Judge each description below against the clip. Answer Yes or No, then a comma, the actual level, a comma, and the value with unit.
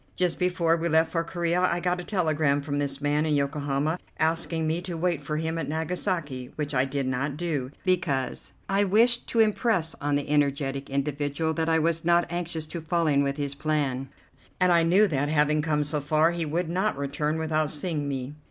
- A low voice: No, medium, 155 Hz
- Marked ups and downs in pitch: No, average, 3.1 semitones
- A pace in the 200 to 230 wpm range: Yes, fast, 205 wpm